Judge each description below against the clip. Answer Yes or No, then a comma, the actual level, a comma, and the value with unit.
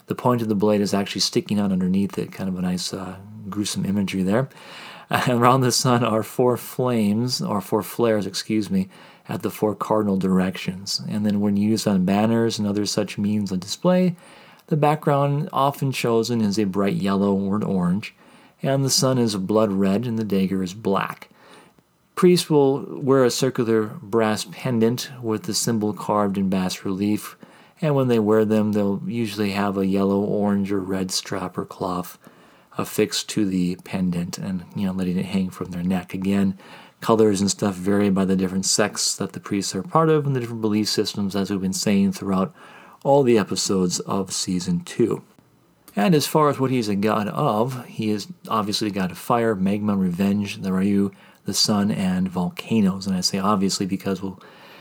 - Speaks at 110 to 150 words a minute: No, average, 190 wpm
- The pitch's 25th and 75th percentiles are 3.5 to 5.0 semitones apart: Yes, average, 4.1 semitones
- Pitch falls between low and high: No, low, 105 Hz